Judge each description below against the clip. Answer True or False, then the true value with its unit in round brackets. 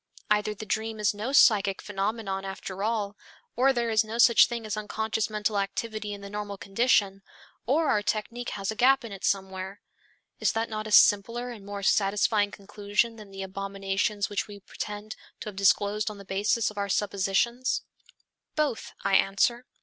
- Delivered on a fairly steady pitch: True (2.1 semitones)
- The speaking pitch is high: True (210 Hz)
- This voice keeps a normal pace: True (180 wpm)